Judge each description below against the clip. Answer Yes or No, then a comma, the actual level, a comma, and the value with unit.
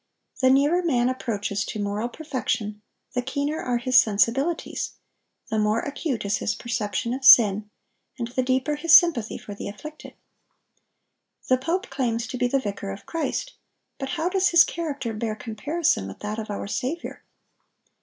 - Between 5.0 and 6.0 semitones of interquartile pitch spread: Yes, wide, 5.5 semitones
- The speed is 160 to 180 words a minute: Yes, average, 165 wpm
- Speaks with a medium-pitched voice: No, very high, 250 Hz